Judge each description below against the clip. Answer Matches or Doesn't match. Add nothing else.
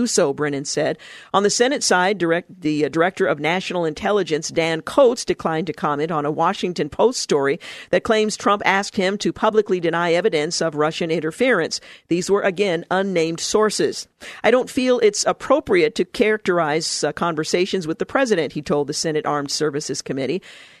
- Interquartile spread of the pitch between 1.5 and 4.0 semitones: Doesn't match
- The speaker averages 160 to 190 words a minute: Matches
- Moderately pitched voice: Matches